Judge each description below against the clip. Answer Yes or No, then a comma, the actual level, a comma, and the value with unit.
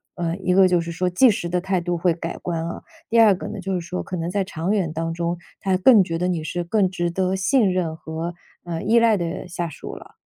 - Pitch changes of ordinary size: No, narrow, 2.2 semitones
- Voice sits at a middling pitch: Yes, medium, 180 Hz